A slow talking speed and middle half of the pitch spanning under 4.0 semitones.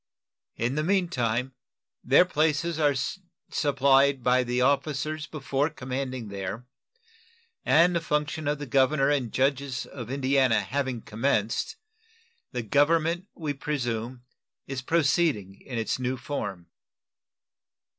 Yes: slow, 120 wpm; average, 3.3 semitones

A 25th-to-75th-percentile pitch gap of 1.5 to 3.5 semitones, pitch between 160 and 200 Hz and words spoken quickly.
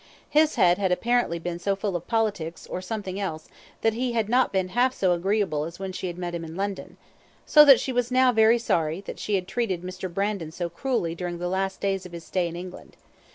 No: average, 4.2 semitones; high, 190 Hz; fast, 235 wpm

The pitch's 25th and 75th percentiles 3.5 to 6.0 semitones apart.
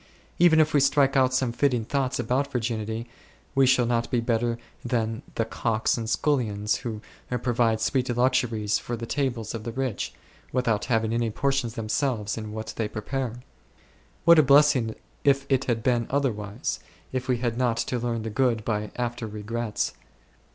No: average, 2.7 semitones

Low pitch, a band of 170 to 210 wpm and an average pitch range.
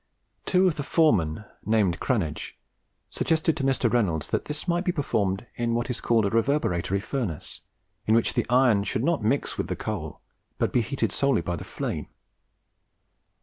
No: low, 120 Hz; average, 175 wpm; wide, 6.3 semitones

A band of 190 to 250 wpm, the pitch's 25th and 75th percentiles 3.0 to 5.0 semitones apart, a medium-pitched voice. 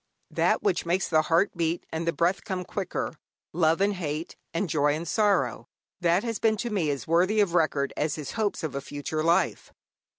Yes: average, 200 wpm; average, 4.0 semitones; medium, 170 Hz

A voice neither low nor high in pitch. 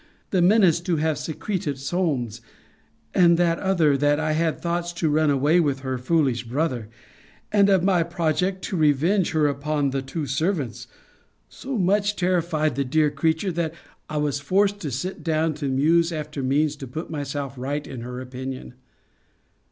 Yes: medium, 155 Hz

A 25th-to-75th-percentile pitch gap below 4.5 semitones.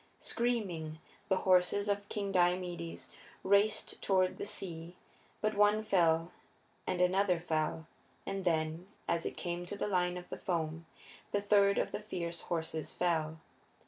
Yes: average, 3.2 semitones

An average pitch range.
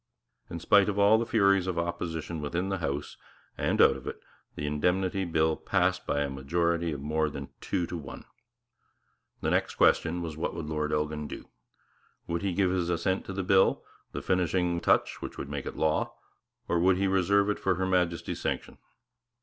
Yes: average, 3.4 semitones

